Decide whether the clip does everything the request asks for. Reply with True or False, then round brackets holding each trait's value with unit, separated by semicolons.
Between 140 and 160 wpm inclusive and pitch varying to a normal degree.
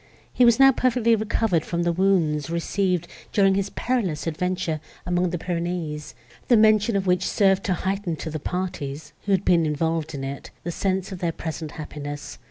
False (180 wpm; 3.5 semitones)